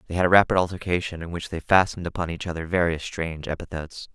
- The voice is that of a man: Yes, male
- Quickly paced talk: Yes, fast, 215 wpm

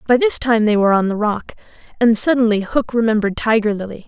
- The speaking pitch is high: Yes, high, 225 Hz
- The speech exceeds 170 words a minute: Yes, fast, 205 wpm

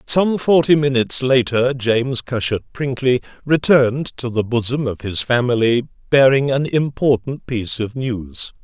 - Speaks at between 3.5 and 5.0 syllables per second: Yes, 4.6 syllables/s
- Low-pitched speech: Yes, low, 125 Hz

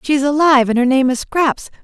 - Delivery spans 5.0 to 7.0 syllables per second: Yes, 5.5 syllables/s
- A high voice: Yes, very high, 275 Hz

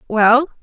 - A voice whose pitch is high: Yes, very high, 250 Hz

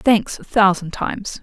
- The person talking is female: Yes, female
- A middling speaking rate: Yes, average, 170 wpm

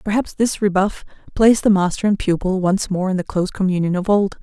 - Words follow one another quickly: Yes, fast, 215 wpm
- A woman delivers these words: Yes, female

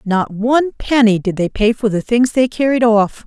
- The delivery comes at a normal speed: No, fast, 220 wpm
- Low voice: No, high, 225 Hz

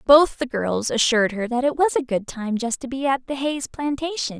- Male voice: No, female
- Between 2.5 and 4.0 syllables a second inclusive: No, 5.2 syllables/s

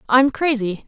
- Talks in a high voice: Yes, high, 245 Hz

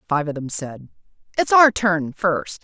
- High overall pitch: No, medium, 165 Hz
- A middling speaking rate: Yes, average, 180 wpm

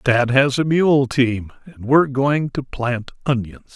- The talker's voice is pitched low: Yes, low, 130 Hz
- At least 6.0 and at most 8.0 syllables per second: No, 4.2 syllables/s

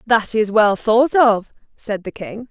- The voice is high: Yes, high, 220 Hz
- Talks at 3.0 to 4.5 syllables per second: Yes, 3.7 syllables/s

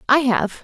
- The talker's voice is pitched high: Yes, high, 245 Hz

